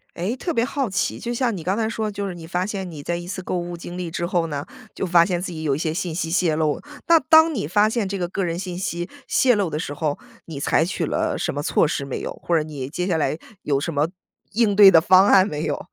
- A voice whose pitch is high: No, medium, 175 Hz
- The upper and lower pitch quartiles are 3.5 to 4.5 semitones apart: Yes, average, 3.8 semitones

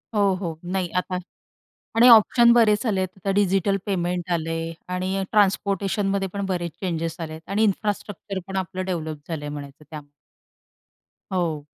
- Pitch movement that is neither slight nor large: Yes, average, 3.2 semitones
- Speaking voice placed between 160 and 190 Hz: Yes, medium, 185 Hz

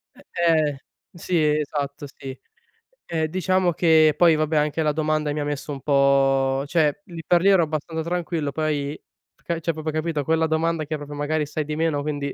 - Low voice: No, medium, 155 Hz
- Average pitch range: No, narrow, 1.9 semitones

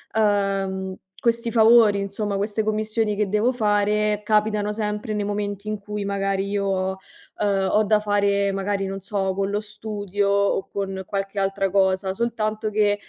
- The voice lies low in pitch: No, high, 205 Hz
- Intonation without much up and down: Yes, narrow, 1.4 semitones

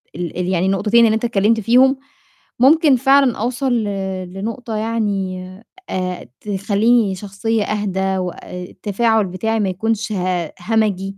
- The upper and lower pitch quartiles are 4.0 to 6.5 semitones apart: No, average, 3.3 semitones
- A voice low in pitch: No, high, 210 Hz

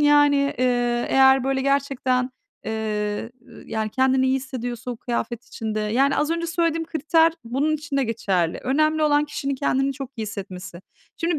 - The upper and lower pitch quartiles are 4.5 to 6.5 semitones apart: No, average, 4.0 semitones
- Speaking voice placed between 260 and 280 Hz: Yes, very high, 265 Hz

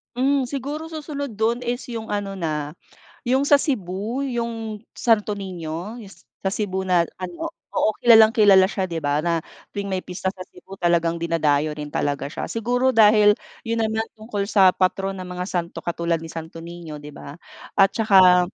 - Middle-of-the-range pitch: No, high, 195 Hz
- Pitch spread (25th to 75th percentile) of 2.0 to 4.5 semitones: No, average, 4.9 semitones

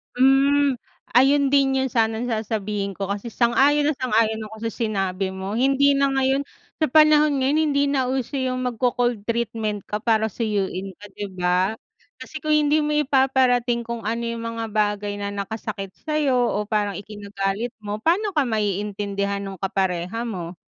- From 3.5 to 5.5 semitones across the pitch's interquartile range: Yes, average, 4.7 semitones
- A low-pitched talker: No, high, 230 Hz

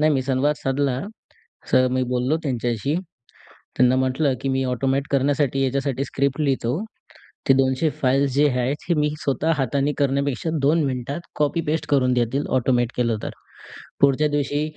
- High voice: No, low, 135 Hz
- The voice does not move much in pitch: Yes, narrow, 2.0 semitones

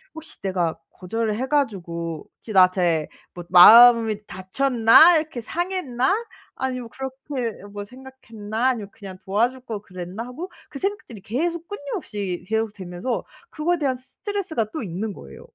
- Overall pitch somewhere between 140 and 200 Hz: No, high, 230 Hz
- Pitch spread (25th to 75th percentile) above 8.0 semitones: No, wide, 5.6 semitones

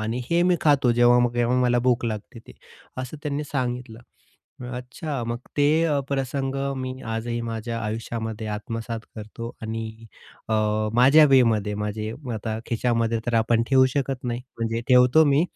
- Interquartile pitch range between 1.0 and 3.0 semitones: Yes, narrow, 2.5 semitones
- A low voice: Yes, low, 120 Hz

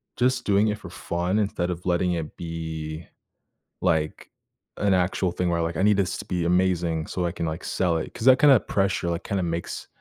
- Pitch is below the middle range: Yes, very low, 90 Hz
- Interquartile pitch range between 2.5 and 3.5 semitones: Yes, average, 2.9 semitones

